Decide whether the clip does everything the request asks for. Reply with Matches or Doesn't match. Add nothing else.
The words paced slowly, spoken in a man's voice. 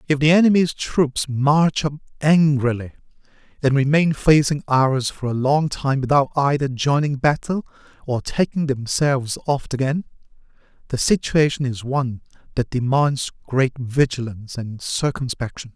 Matches